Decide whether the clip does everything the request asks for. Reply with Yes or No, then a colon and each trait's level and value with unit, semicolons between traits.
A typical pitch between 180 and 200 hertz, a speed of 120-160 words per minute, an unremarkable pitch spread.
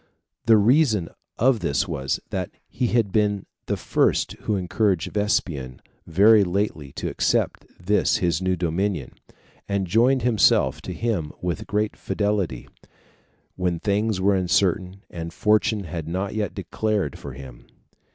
No: low, 100 Hz; average, 140 wpm; average, 3.9 semitones